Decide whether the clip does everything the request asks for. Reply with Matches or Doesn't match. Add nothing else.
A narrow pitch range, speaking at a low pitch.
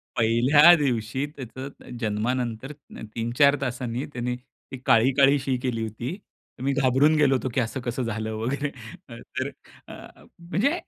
Doesn't match